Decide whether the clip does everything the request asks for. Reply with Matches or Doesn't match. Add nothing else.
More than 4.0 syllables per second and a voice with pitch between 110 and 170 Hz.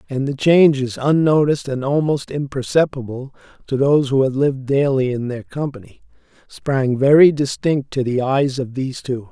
Matches